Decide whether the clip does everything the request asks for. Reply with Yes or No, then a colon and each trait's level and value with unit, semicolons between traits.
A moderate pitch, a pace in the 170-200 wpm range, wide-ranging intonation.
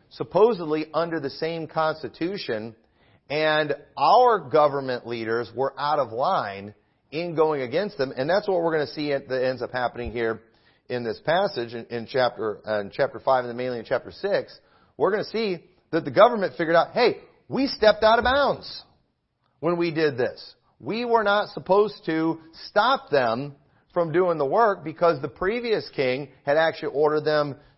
Yes: medium, 155 Hz; average, 175 wpm; wide, 6.1 semitones